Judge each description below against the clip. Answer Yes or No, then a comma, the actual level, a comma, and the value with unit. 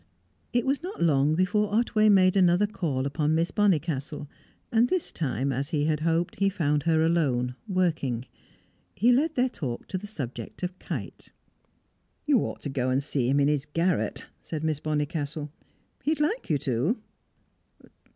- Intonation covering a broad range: Yes, wide, 5.7 semitones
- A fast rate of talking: No, average, 170 wpm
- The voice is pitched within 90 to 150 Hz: No, medium, 160 Hz